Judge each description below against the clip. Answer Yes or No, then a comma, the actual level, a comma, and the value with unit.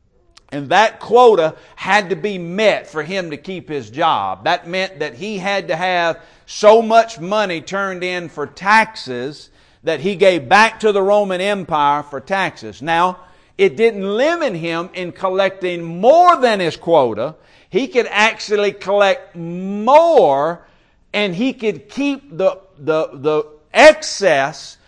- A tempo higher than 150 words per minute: No, average, 145 wpm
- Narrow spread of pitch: No, average, 4.2 semitones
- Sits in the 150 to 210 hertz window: Yes, high, 190 Hz